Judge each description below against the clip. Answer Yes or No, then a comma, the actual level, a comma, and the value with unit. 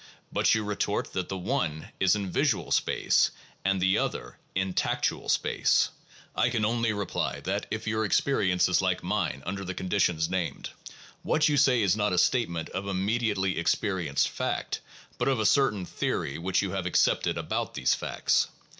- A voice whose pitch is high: No, very low, 95 Hz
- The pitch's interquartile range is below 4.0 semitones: Yes, average, 3.3 semitones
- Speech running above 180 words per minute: No, average, 175 wpm